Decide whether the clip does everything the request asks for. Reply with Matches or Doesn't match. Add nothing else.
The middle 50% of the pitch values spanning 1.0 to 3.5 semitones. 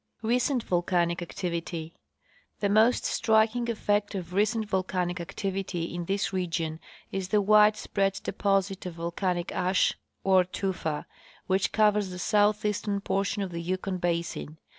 Matches